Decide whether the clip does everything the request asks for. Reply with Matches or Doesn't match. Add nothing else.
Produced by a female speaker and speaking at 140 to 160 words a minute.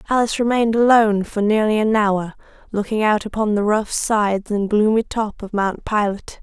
Doesn't match